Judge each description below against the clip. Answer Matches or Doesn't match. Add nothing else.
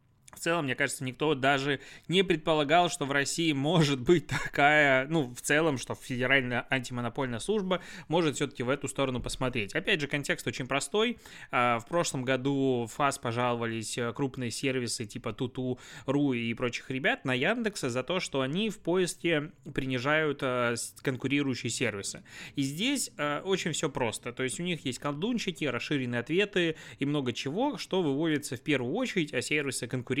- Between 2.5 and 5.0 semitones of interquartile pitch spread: Matches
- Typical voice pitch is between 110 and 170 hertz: Matches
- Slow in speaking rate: Doesn't match